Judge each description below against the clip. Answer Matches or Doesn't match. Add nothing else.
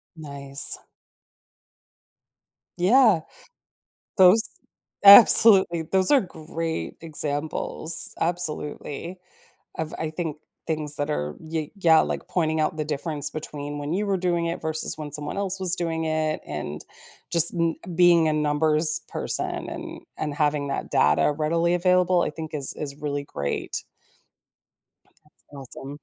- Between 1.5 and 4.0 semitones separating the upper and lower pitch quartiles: Matches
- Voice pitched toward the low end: Doesn't match